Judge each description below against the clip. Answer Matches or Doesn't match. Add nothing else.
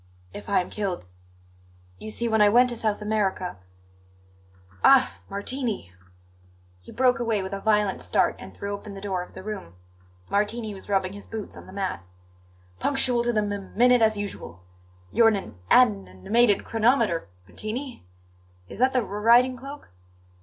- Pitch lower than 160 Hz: Doesn't match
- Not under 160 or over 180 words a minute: Matches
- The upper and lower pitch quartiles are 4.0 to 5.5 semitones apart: Doesn't match